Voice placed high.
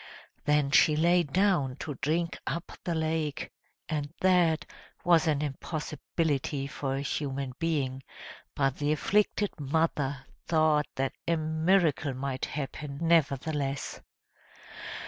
No: medium, 150 Hz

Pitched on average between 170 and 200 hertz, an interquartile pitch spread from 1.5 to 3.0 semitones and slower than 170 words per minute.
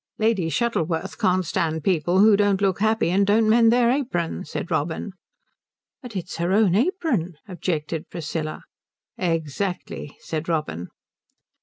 No: medium, 185 Hz; average, 4.9 semitones; slow, 135 wpm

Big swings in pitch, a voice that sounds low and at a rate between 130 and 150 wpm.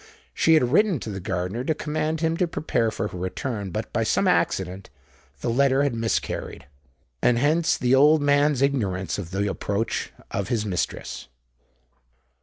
No: wide, 7.0 semitones; low, 120 Hz; average, 160 wpm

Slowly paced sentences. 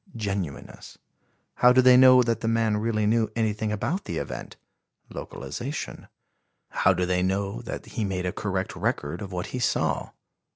No: average, 165 wpm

